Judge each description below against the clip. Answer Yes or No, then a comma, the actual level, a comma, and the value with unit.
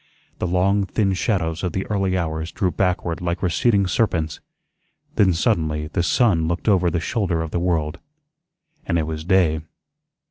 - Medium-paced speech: Yes, average, 165 wpm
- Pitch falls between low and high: No, very low, 90 Hz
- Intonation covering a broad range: No, average, 2.9 semitones